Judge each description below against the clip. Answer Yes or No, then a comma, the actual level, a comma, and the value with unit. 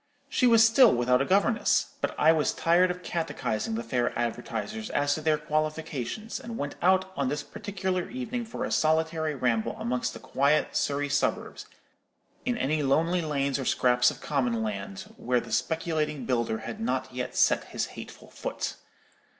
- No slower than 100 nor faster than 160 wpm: No, average, 170 wpm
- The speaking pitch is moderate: Yes, medium, 150 Hz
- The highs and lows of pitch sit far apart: Yes, wide, 6.1 semitones